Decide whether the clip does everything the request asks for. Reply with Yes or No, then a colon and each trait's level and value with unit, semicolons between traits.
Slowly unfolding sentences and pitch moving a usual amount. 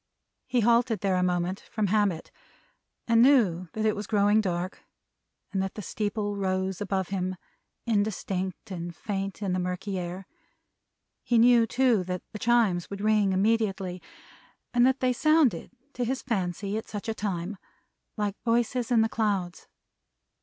No: average, 155 wpm; average, 3.4 semitones